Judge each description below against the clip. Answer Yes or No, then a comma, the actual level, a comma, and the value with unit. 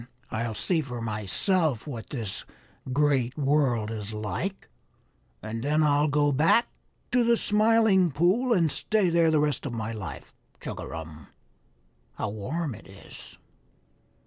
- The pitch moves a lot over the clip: Yes, wide, 7.4 semitones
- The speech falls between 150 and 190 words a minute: No, slow, 135 wpm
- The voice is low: No, medium, 145 Hz